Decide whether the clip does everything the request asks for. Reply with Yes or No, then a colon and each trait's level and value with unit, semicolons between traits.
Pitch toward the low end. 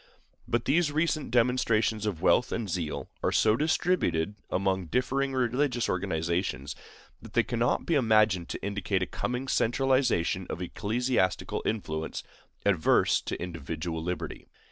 Yes: low, 110 Hz